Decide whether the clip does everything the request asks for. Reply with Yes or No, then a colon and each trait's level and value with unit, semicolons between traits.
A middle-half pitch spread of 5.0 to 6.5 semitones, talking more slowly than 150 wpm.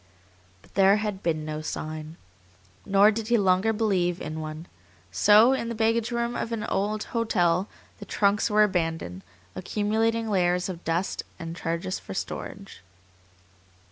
No: average, 4.6 semitones; average, 140 wpm